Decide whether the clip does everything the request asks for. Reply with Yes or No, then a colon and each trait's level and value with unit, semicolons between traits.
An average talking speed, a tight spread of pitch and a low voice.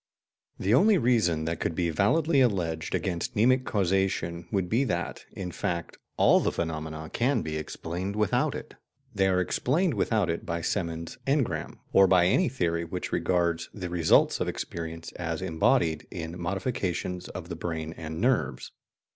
No: average, 160 wpm; average, 4.2 semitones; very low, 90 Hz